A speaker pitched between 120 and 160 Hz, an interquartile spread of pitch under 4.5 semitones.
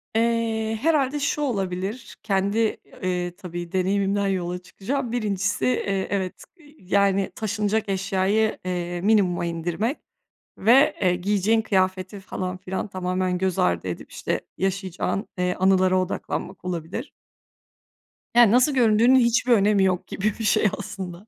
No: high, 195 Hz; average, 3.3 semitones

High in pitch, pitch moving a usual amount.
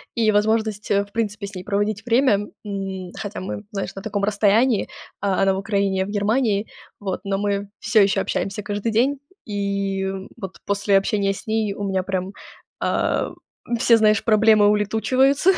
No: high, 205 Hz; narrow, 1.7 semitones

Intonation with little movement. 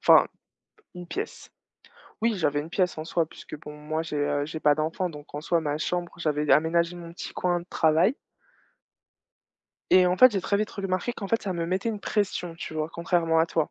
No: average, 3.0 semitones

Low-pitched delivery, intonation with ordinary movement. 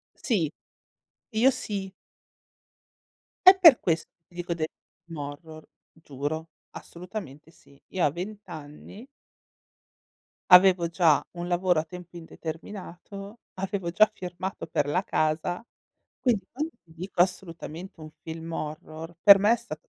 No: medium, 175 Hz; average, 3.4 semitones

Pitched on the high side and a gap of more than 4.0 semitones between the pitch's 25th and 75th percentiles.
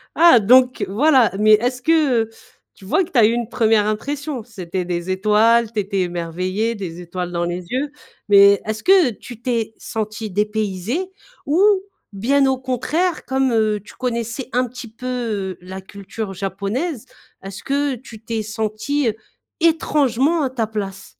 Yes: high, 225 Hz; average, 4.5 semitones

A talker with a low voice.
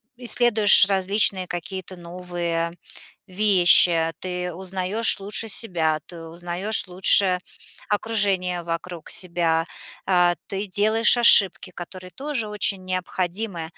No: medium, 185 Hz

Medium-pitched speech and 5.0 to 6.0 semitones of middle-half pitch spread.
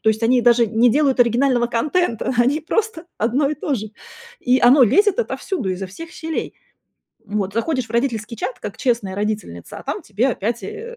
No: high, 240 Hz; wide, 5.4 semitones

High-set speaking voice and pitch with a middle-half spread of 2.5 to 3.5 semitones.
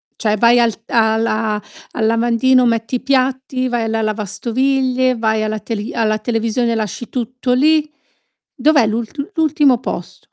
Yes: high, 235 Hz; average, 2.8 semitones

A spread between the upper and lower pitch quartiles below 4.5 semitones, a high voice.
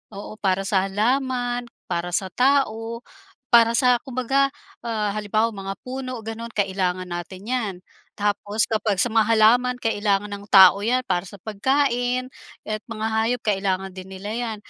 Yes: average, 3.7 semitones; high, 220 Hz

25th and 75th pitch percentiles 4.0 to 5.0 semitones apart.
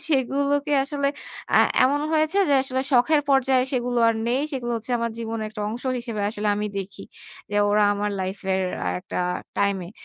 Yes: average, 4.6 semitones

